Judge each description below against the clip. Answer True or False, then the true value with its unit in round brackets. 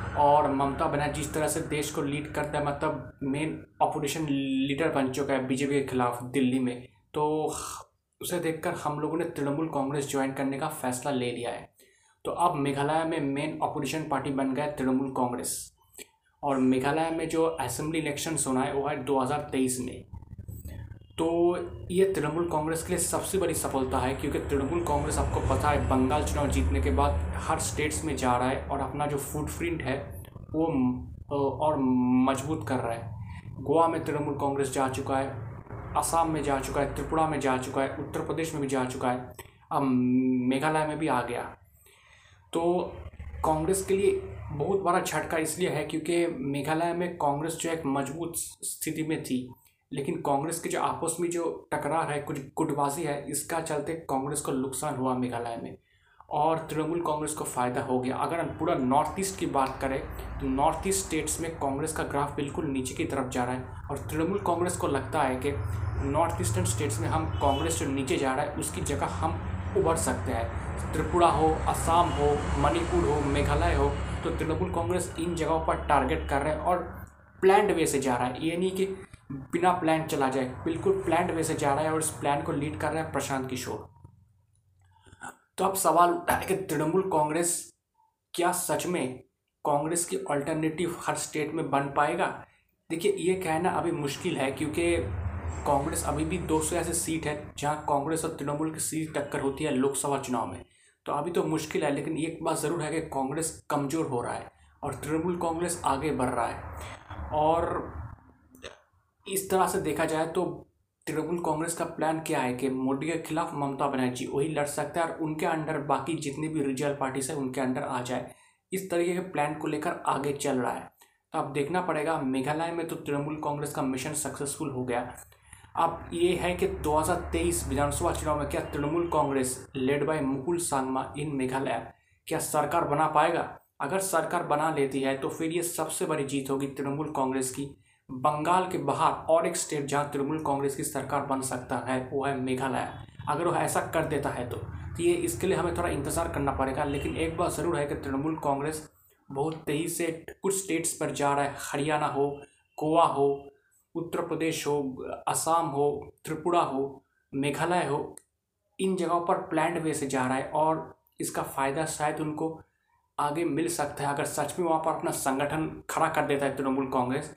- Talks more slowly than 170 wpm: False (190 wpm)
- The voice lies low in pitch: False (145 Hz)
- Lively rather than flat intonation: False (3.3 semitones)